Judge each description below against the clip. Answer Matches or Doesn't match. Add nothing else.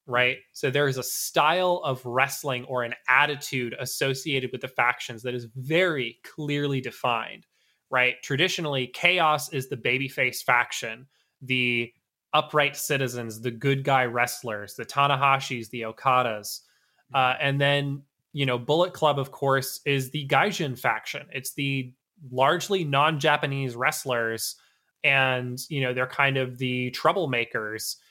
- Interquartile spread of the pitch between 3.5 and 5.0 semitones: Doesn't match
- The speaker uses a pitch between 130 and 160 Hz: Matches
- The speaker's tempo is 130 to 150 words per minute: Matches